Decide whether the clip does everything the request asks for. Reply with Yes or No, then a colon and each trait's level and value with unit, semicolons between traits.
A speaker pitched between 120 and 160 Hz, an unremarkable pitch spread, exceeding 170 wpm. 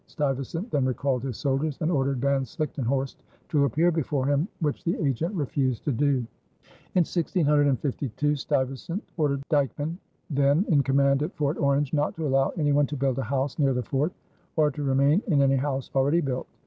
No: medium, 140 Hz; narrow, 2.0 semitones; average, 180 wpm